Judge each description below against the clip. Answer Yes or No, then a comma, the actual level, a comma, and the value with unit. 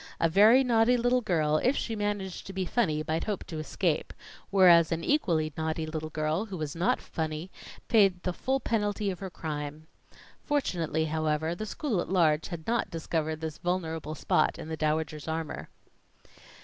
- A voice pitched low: No, medium, 170 Hz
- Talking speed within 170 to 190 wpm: Yes, average, 175 wpm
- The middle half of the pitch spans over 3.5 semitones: Yes, average, 4.5 semitones